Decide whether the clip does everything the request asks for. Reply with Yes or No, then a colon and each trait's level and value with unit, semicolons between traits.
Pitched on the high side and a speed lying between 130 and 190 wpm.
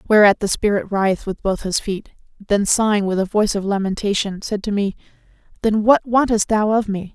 No: high, 205 Hz; average, 200 wpm